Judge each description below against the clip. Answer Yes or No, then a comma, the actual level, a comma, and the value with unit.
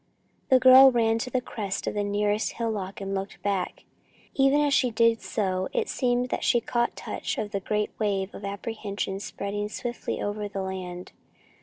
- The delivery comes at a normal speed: Yes, average, 180 wpm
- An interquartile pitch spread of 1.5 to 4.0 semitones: Yes, average, 3.3 semitones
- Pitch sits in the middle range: No, high, 210 Hz